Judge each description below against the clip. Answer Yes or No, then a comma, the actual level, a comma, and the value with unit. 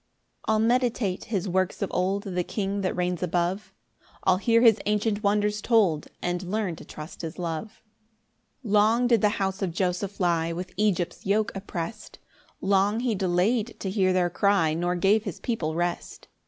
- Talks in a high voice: Yes, high, 195 Hz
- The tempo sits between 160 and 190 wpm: Yes, average, 175 wpm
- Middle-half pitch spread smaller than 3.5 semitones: Yes, average, 3.0 semitones